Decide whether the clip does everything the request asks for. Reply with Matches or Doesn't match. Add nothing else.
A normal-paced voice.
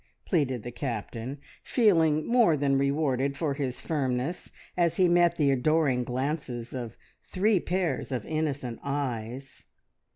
Doesn't match